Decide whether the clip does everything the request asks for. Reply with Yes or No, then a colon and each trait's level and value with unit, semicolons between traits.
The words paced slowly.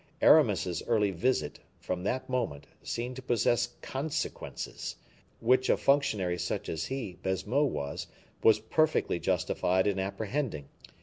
Yes: slow, 125 wpm